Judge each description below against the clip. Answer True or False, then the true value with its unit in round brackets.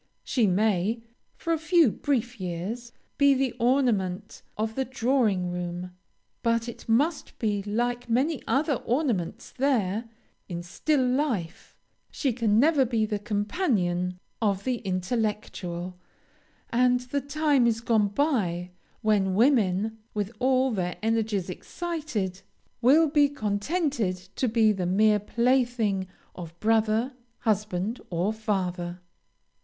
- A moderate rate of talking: False (125 wpm)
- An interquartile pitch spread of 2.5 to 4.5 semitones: False (5.1 semitones)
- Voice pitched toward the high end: True (225 Hz)